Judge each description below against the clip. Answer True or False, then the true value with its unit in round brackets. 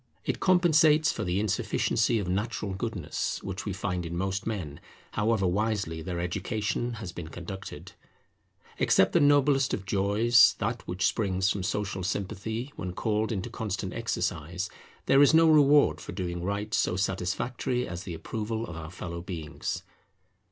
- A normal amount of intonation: True (4.2 semitones)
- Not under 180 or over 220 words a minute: False (155 wpm)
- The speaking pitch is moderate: False (100 Hz)